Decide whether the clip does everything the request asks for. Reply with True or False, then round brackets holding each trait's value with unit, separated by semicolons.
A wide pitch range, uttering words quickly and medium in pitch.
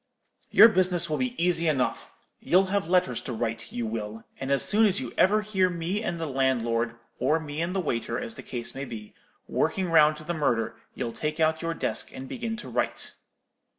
True (6.3 semitones; 210 wpm; 160 Hz)